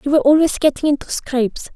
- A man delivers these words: No, female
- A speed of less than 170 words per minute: No, fast, 205 wpm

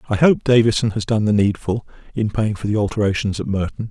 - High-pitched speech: No, low, 105 Hz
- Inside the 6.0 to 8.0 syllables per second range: Yes, 6.1 syllables/s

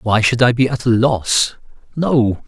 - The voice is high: No, low, 120 Hz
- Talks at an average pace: Yes, average, 195 wpm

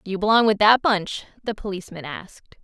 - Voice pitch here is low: No, high, 200 Hz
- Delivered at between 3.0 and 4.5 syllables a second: No, 6.4 syllables/s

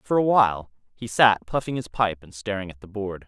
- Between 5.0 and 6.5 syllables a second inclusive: Yes, 5.5 syllables/s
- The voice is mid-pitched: No, low, 105 Hz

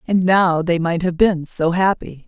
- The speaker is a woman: Yes, female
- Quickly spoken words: Yes, fast, 210 wpm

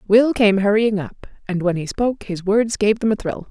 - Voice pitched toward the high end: Yes, high, 205 Hz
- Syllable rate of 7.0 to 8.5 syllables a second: No, 5.1 syllables/s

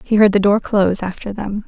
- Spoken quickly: Yes, fast, 250 wpm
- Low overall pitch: No, high, 205 Hz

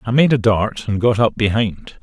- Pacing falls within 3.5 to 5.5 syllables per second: Yes, 4.7 syllables/s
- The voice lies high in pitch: No, low, 110 Hz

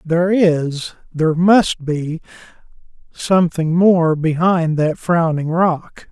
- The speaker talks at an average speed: No, slow, 90 wpm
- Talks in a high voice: No, medium, 165 Hz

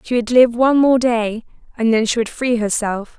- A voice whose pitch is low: No, high, 235 Hz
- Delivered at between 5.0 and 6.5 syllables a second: Yes, 5.1 syllables/s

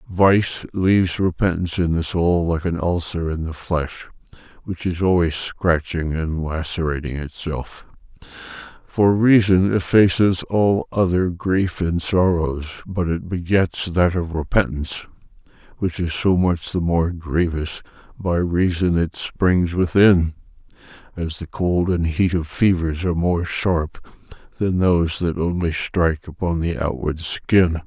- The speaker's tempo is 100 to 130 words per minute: No, average, 140 wpm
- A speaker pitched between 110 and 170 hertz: No, very low, 85 Hz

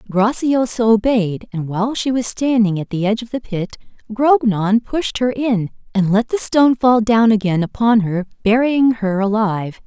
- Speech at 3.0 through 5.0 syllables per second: Yes, 4.8 syllables/s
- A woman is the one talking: Yes, female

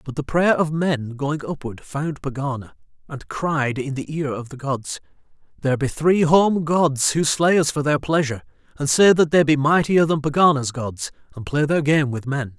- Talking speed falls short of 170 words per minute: No, fast, 205 wpm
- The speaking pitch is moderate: Yes, medium, 145 Hz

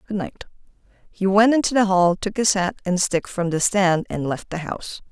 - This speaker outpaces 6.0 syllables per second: No, 5.2 syllables/s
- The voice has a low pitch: No, high, 190 Hz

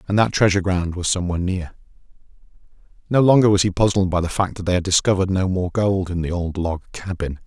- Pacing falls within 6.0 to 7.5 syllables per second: Yes, 6.5 syllables/s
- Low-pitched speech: Yes, very low, 95 Hz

